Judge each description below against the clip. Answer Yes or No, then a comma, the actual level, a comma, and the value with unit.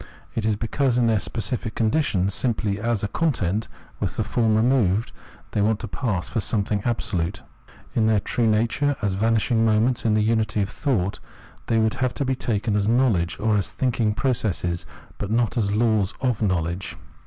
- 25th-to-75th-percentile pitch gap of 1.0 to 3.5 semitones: Yes, narrow, 2.6 semitones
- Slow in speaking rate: No, average, 180 wpm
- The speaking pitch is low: Yes, low, 110 Hz